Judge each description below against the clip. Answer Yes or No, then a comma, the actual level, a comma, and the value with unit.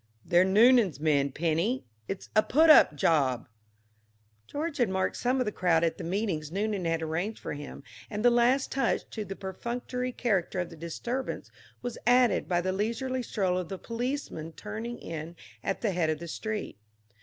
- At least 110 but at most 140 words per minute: No, average, 180 wpm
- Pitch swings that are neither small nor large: No, wide, 6.3 semitones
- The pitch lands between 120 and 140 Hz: No, high, 195 Hz